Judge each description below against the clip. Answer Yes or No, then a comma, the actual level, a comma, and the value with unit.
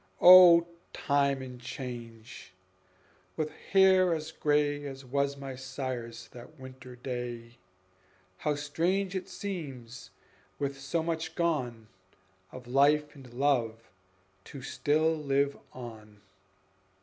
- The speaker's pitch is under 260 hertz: Yes, medium, 140 Hz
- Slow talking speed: Yes, slow, 110 wpm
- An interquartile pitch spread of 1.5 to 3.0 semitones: No, average, 3.8 semitones